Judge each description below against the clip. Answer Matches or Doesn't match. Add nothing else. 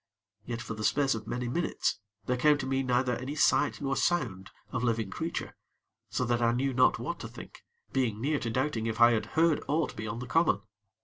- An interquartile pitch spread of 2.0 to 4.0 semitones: Matches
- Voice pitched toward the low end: Matches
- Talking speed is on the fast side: Matches